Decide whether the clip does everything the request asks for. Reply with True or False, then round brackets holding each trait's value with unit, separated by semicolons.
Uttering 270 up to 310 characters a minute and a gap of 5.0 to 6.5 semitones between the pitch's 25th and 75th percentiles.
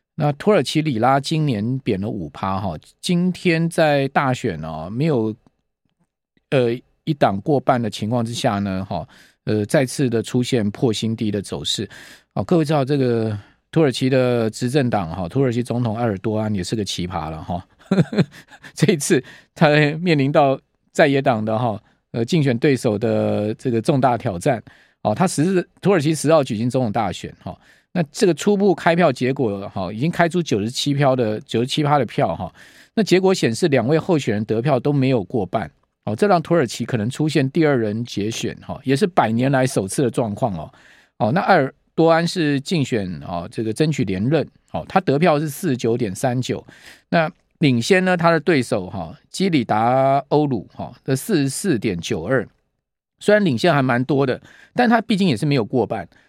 True (275 characters per minute; 5.6 semitones)